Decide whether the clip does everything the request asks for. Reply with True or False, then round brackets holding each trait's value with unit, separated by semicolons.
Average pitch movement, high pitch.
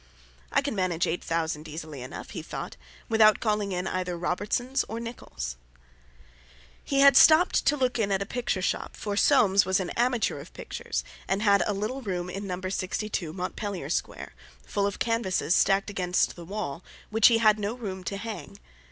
True (3.8 semitones; 200 Hz)